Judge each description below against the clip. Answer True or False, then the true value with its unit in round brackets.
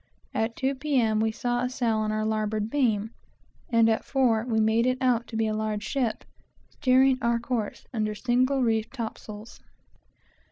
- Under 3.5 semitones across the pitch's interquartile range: True (2.6 semitones)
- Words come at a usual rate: True (170 wpm)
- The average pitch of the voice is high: True (230 Hz)